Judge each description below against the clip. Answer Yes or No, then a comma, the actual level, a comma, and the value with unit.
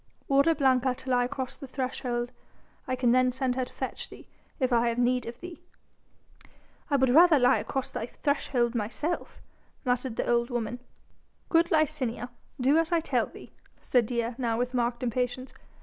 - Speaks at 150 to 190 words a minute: Yes, average, 175 wpm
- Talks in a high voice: Yes, very high, 255 Hz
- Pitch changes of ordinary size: No, narrow, 2.1 semitones